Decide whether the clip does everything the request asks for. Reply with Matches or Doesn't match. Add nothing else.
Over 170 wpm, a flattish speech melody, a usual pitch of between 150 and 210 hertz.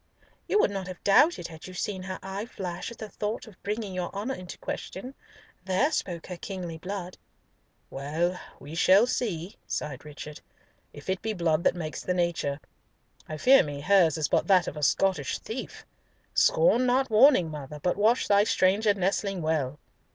Doesn't match